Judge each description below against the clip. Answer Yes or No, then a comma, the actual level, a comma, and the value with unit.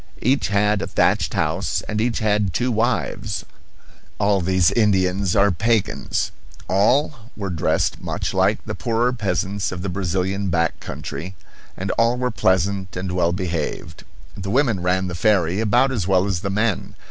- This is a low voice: Yes, low, 100 Hz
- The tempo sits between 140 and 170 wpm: Yes, average, 160 wpm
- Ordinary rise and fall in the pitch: Yes, average, 3.1 semitones